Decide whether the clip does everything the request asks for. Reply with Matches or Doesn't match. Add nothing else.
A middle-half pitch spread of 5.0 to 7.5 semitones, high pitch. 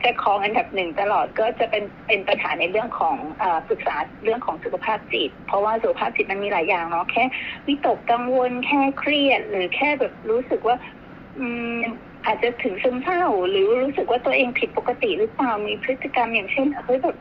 Doesn't match